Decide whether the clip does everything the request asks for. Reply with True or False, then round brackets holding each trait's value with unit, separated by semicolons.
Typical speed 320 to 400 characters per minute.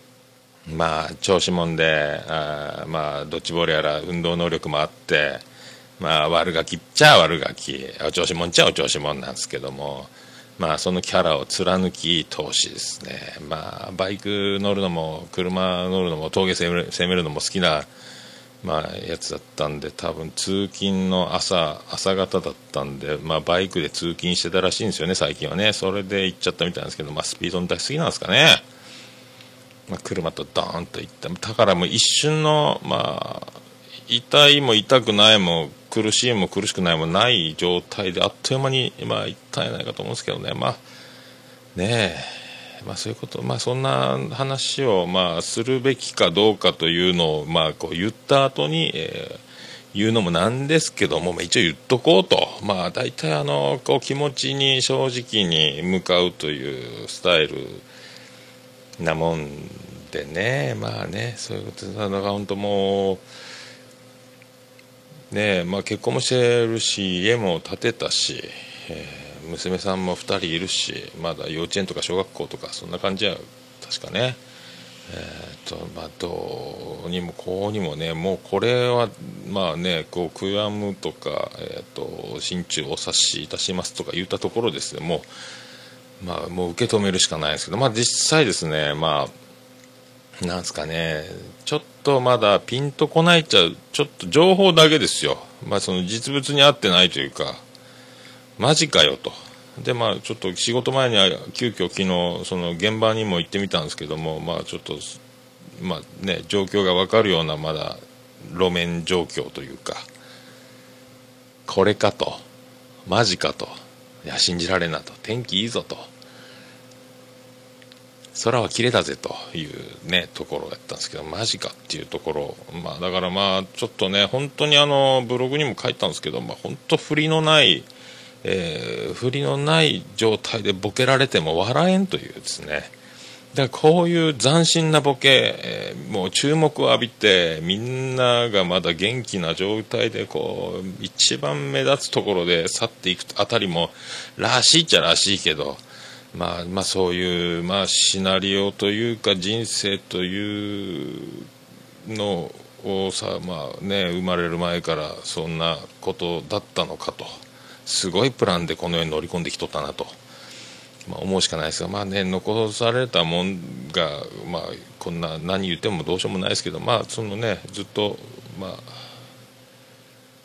False (305 characters per minute)